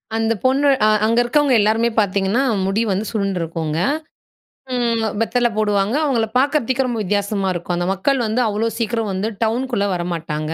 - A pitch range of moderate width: Yes, average, 3.7 semitones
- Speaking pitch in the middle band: No, high, 220 Hz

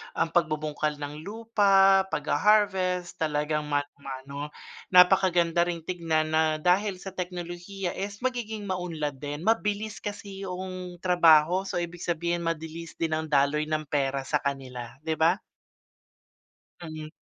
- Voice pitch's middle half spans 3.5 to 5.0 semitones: Yes, average, 3.8 semitones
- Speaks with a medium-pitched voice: Yes, medium, 170 Hz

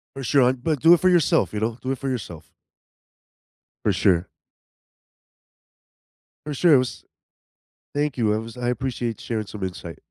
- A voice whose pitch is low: Yes, low, 125 Hz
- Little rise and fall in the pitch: No, average, 4.3 semitones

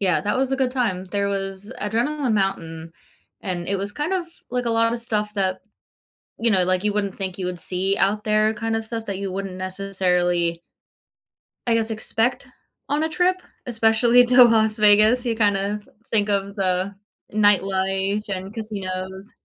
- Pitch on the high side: Yes, high, 205 Hz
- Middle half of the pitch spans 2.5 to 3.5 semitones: Yes, average, 3.0 semitones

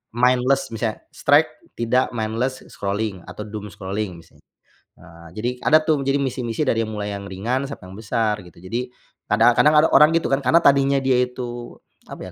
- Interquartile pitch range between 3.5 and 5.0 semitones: Yes, average, 3.8 semitones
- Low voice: Yes, low, 115 Hz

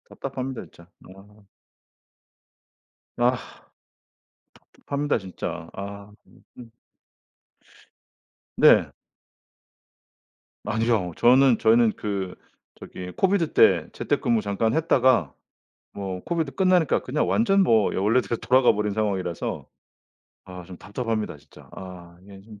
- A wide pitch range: No, average, 4.9 semitones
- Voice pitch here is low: Yes, low, 110 Hz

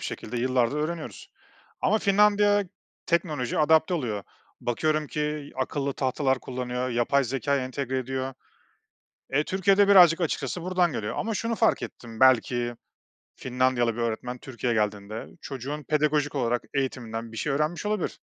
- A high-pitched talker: No, low, 135 Hz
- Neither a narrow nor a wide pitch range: Yes, average, 4.5 semitones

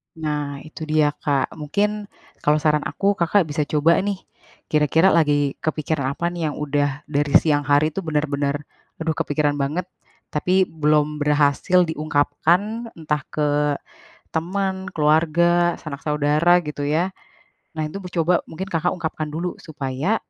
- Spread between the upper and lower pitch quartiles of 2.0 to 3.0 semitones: Yes, average, 2.7 semitones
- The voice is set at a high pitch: No, medium, 155 Hz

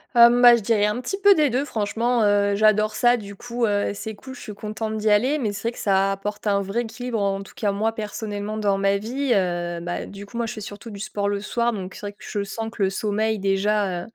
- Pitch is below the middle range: No, high, 210 Hz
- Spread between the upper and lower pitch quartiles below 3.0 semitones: Yes, narrow, 2.6 semitones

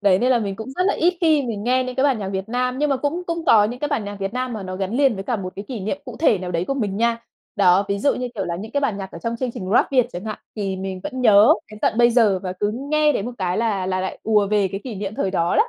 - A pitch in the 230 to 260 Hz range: No, high, 220 Hz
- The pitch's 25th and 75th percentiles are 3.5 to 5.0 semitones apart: Yes, average, 4.7 semitones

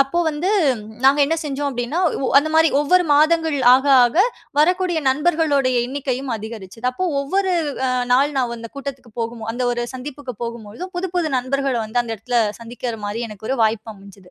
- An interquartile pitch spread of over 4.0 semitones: Yes, average, 4.5 semitones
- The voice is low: No, very high, 265 Hz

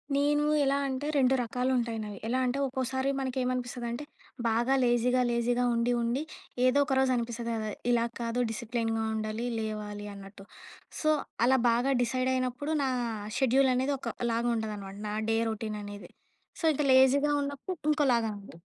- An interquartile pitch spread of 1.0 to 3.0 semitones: Yes, average, 2.7 semitones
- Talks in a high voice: Yes, high, 245 Hz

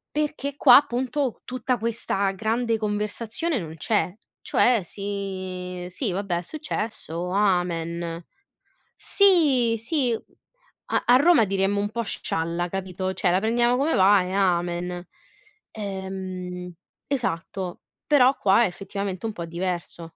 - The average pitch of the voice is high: Yes, high, 200 Hz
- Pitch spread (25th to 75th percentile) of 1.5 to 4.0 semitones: No, average, 4.9 semitones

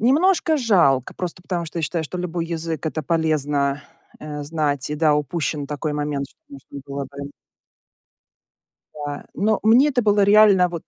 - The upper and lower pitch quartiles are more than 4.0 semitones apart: Yes, average, 5.1 semitones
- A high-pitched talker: No, medium, 160 Hz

